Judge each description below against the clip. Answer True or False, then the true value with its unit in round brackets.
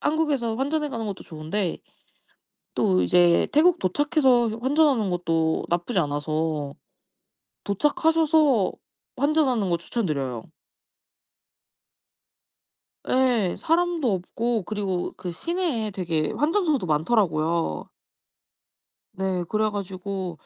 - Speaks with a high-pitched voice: True (210 Hz)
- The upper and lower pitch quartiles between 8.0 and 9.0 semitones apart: True (8.7 semitones)